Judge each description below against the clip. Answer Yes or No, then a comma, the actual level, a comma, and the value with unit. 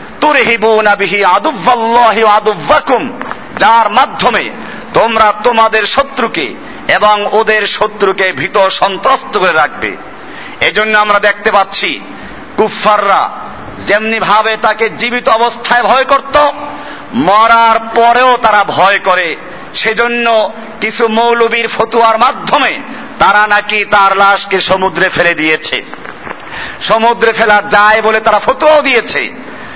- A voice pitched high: Yes, high, 220 Hz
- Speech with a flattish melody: Yes, narrow, 2.3 semitones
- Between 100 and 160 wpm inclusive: No, average, 85 wpm